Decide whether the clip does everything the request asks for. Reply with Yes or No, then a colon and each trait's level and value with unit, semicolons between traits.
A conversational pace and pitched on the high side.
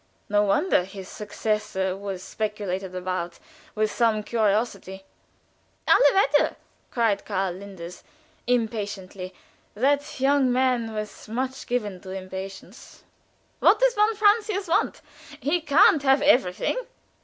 No: slow, 115 wpm; high, 215 Hz